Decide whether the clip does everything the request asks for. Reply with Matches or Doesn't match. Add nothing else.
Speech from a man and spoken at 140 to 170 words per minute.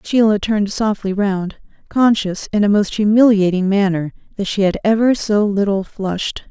Doesn't match